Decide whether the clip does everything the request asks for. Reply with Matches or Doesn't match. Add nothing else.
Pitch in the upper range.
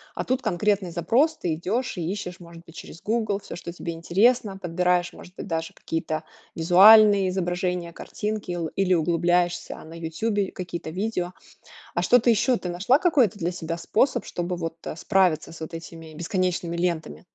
Doesn't match